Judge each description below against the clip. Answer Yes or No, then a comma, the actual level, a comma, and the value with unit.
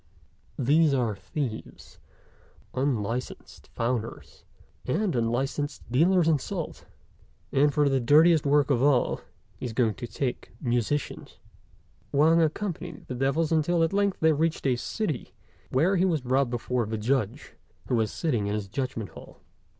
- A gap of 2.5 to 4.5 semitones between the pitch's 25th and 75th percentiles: No, average, 4.9 semitones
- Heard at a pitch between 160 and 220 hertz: No, low, 135 Hz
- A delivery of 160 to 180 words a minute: No, average, 145 wpm